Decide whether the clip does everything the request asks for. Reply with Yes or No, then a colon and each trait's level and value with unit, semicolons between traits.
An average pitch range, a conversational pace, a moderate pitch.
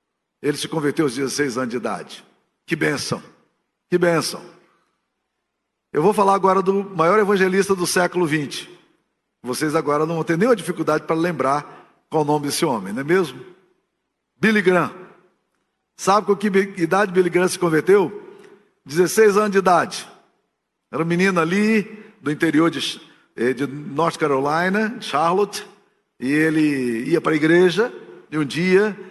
Yes: average, 4.2 semitones; average, 150 wpm; medium, 175 Hz